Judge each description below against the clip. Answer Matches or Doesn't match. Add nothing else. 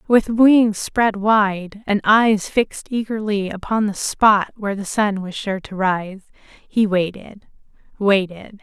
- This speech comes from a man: Doesn't match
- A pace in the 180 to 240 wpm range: Doesn't match